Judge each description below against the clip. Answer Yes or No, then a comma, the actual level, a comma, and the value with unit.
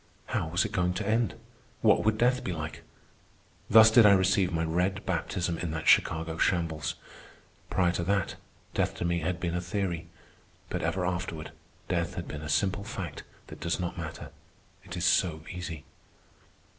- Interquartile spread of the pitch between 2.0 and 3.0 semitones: Yes, narrow, 2.6 semitones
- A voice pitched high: No, very low, 90 Hz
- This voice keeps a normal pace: Yes, average, 175 wpm